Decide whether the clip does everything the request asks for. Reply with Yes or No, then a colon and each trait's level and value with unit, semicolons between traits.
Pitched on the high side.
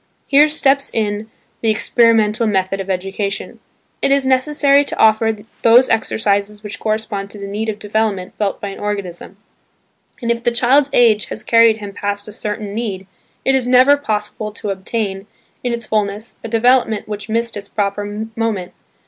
Yes: high, 215 Hz